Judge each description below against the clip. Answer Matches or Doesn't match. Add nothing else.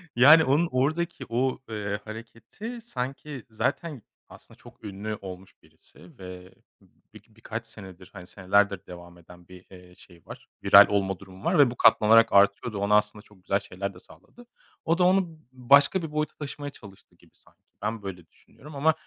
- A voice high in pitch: Doesn't match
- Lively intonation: Matches